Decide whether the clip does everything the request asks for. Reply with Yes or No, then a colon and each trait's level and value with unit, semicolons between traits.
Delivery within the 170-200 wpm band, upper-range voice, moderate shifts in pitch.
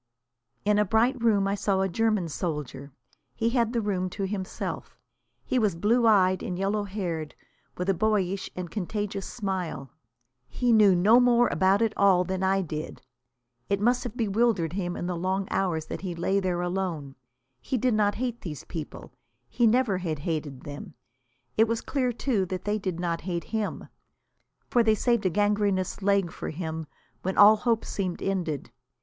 Yes: average, 180 wpm; high, 195 Hz; average, 3.6 semitones